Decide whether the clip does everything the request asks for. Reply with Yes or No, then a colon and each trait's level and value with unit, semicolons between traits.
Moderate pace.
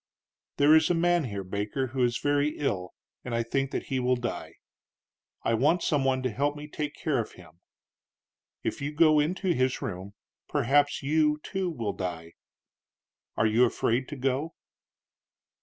Yes: average, 170 wpm